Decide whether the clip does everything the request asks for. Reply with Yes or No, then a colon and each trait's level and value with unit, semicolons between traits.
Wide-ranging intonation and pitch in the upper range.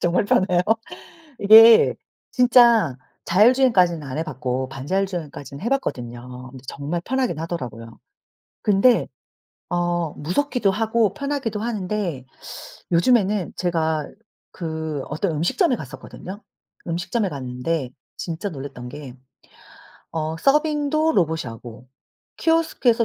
No: wide, 7.8 semitones; medium, 175 Hz